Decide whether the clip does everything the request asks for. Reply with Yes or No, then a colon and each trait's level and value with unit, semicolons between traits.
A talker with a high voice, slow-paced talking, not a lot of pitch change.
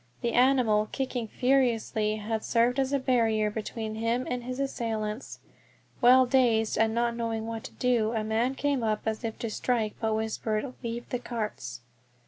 No: high, 230 Hz; average, 170 wpm; narrow, 2.2 semitones